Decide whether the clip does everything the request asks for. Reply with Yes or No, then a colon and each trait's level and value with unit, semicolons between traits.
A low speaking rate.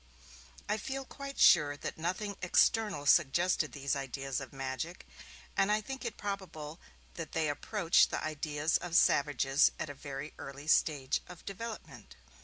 No: average, 150 wpm